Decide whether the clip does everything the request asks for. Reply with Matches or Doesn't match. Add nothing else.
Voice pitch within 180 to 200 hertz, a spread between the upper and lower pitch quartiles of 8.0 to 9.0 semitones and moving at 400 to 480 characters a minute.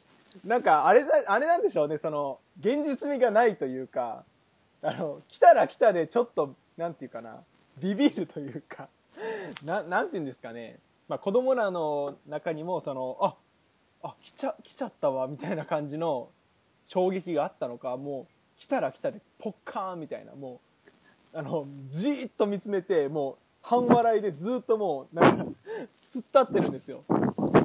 Doesn't match